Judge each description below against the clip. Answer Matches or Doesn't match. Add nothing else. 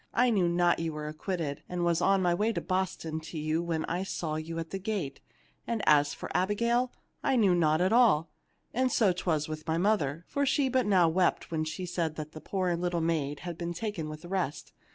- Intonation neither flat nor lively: Matches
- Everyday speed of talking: Doesn't match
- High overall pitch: Doesn't match